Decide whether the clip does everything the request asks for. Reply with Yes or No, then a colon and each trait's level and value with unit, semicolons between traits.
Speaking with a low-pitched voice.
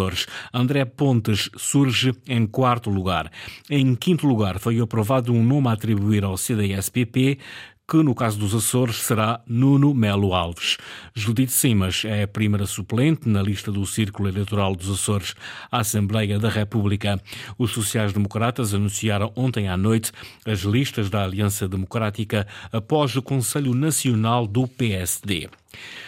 Yes: low, 110 Hz